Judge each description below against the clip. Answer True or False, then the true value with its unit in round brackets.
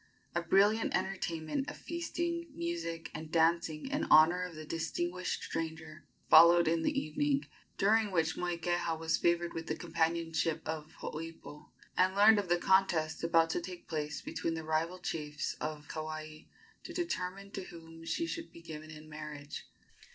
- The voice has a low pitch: False (165 Hz)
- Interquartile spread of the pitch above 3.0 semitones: False (2.7 semitones)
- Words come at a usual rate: True (160 wpm)